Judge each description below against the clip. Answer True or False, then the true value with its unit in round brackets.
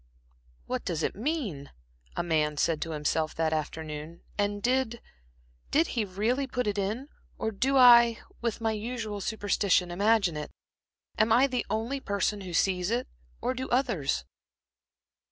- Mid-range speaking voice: False (205 Hz)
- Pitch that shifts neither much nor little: False (6.0 semitones)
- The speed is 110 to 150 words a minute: True (145 wpm)